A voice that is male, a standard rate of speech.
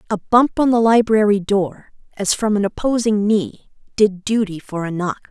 No: female; average, 180 wpm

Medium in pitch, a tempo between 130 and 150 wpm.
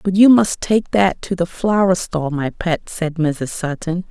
No: medium, 175 Hz; fast, 205 wpm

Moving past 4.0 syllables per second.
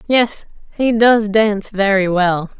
No: 3.9 syllables/s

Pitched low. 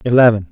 Yes: low, 115 Hz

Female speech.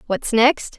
Yes: female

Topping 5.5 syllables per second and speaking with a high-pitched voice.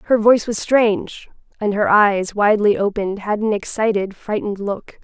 No: 5.3 syllables/s; high, 210 Hz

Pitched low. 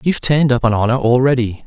Yes: low, 125 Hz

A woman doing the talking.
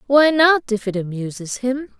Yes: female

